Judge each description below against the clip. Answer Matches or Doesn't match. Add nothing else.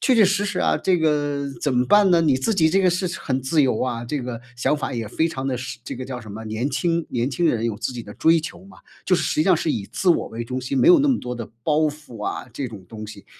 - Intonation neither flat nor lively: Doesn't match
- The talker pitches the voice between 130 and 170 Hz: Matches